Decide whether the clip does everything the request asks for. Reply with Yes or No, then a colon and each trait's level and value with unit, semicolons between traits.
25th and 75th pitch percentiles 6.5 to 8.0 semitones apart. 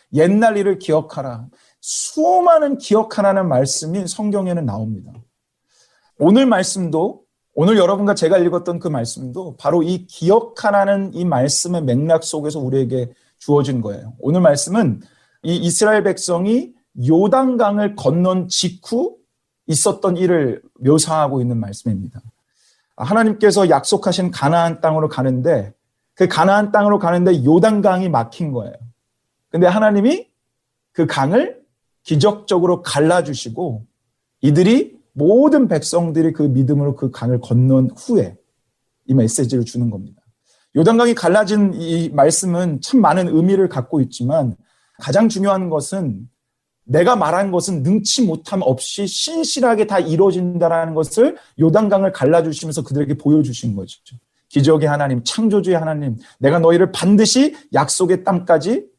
Yes: wide, 6.9 semitones